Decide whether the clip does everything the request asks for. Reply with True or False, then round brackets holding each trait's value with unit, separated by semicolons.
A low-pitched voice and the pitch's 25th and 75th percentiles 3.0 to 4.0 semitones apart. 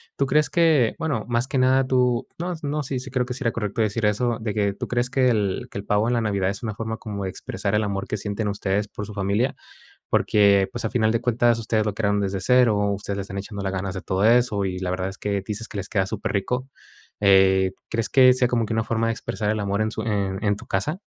True (110 Hz; 3.4 semitones)